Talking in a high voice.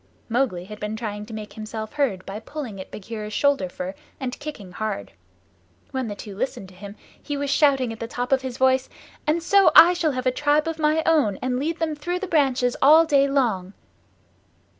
Yes: very high, 255 Hz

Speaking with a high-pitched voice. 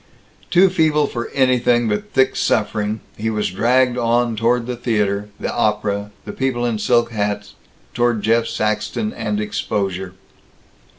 No: low, 115 Hz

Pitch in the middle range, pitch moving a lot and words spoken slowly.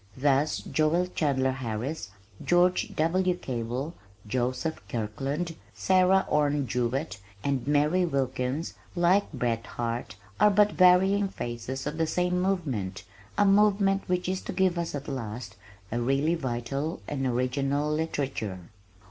Yes: medium, 145 Hz; wide, 5.9 semitones; slow, 130 wpm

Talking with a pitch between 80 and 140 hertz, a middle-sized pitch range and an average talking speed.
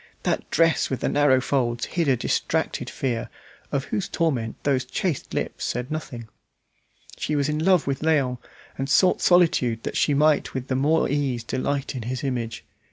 Yes: low, 135 Hz; average, 3.5 semitones; average, 175 wpm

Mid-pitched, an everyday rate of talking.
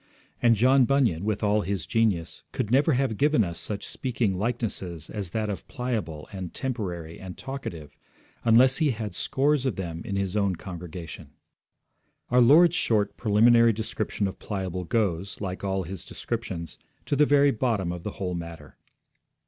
No: low, 105 Hz; average, 165 wpm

